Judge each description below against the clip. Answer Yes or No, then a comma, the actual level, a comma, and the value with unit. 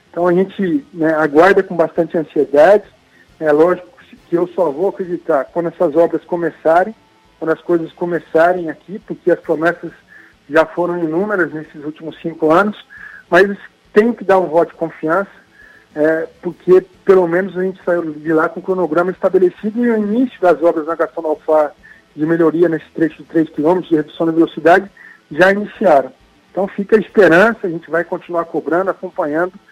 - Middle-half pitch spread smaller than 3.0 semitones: Yes, narrow, 2.6 semitones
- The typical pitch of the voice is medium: Yes, medium, 175 Hz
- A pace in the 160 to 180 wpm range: Yes, average, 170 wpm